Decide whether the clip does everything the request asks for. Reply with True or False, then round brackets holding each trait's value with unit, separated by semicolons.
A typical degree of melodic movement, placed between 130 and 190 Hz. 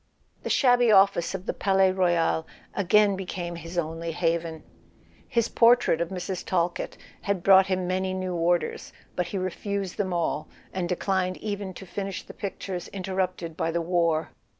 False (2.1 semitones; 185 Hz)